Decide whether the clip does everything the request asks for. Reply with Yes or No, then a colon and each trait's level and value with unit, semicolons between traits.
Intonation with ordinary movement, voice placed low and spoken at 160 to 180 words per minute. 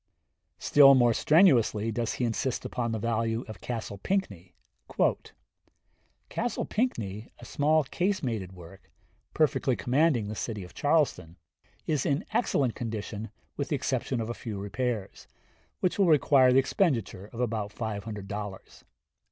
No: average, 4.9 semitones; low, 115 Hz; average, 140 wpm